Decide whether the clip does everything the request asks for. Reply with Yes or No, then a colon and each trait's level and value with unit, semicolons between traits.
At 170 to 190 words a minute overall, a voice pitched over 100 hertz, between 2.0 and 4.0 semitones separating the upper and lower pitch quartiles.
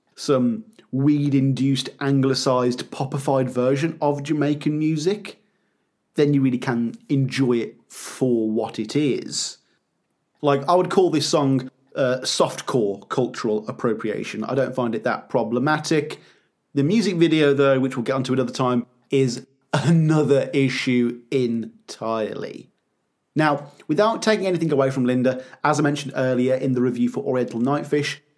No: average, 140 wpm; low, 135 Hz; average, 2.9 semitones